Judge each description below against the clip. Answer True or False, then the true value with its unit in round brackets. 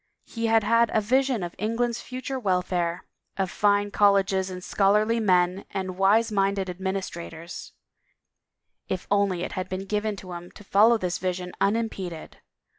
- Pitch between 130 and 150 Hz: False (195 Hz)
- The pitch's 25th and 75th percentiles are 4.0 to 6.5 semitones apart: False (2.9 semitones)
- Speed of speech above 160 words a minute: False (155 wpm)